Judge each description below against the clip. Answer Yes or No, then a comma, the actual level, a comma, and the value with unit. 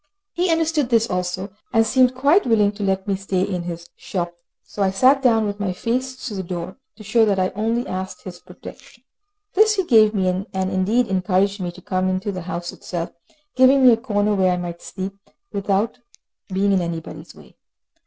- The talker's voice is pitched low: No, high, 200 Hz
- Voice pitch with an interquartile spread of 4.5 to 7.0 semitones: No, average, 3.9 semitones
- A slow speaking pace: No, average, 200 wpm